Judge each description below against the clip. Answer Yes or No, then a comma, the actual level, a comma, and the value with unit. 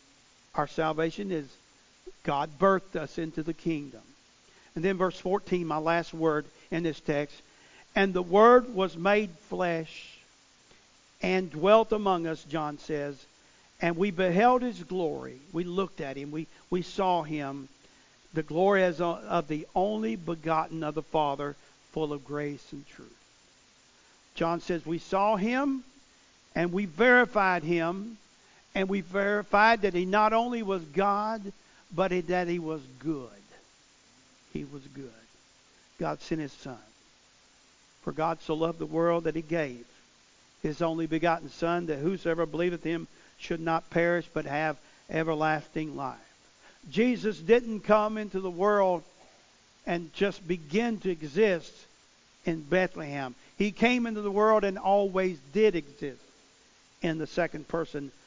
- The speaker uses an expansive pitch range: No, average, 4.0 semitones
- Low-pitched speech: No, medium, 170 Hz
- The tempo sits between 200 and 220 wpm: No, average, 145 wpm